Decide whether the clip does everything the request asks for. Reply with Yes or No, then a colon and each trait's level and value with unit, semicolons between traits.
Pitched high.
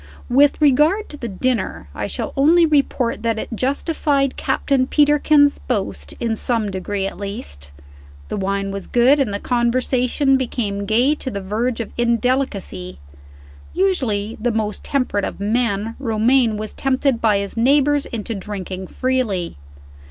Yes: high, 235 Hz